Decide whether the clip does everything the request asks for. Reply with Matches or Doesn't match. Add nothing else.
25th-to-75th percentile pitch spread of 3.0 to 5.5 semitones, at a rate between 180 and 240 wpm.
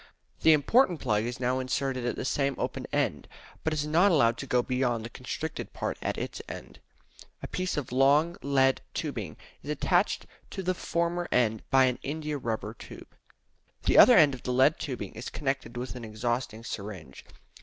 Matches